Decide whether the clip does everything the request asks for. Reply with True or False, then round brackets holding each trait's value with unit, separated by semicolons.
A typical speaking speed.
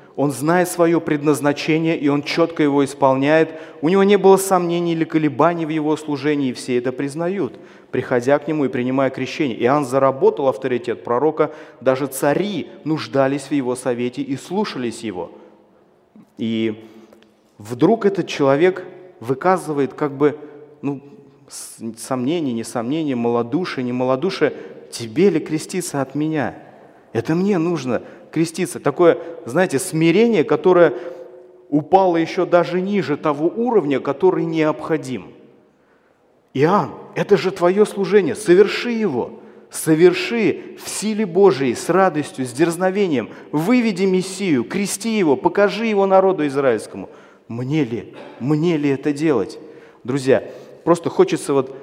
True (125 wpm)